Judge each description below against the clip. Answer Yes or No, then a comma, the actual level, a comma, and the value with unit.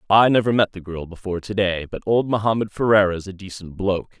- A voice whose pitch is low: Yes, low, 100 Hz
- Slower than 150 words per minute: No, average, 200 wpm